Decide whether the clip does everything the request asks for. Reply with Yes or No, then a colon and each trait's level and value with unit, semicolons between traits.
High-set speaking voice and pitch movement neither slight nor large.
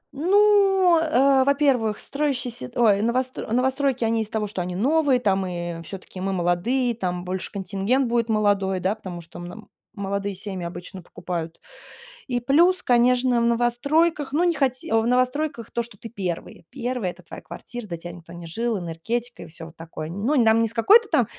No: high, 230 Hz; wide, 5.8 semitones